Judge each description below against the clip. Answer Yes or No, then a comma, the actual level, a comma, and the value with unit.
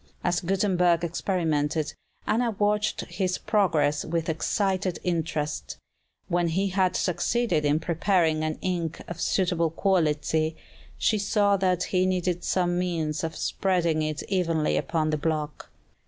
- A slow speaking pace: Yes, slow, 130 wpm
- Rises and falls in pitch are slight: No, average, 3.0 semitones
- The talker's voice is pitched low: No, medium, 175 Hz